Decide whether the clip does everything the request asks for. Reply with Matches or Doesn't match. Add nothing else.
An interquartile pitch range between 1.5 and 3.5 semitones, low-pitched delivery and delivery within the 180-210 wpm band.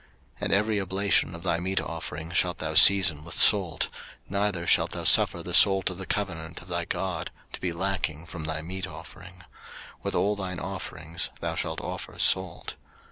Matches